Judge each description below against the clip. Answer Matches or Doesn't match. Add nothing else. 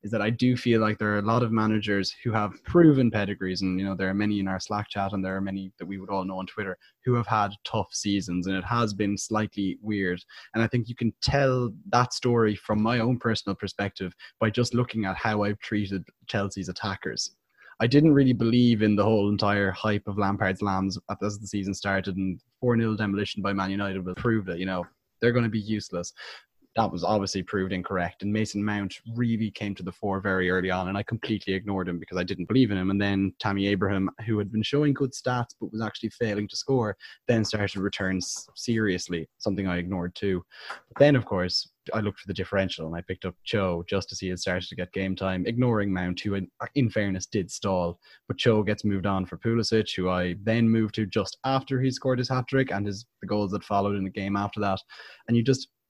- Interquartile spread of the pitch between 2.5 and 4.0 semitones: Matches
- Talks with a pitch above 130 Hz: Doesn't match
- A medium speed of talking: Doesn't match